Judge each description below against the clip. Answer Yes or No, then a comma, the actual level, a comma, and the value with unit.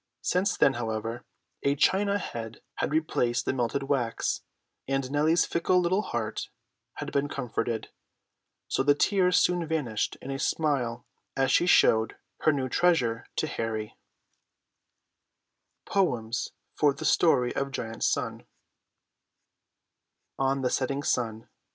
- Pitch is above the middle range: No, low, 135 Hz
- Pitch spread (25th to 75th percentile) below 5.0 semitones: No, wide, 5.5 semitones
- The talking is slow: Yes, slow, 110 wpm